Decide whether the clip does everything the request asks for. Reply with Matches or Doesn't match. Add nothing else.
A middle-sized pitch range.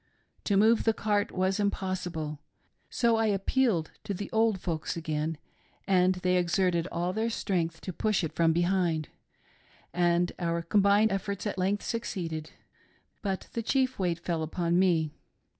Matches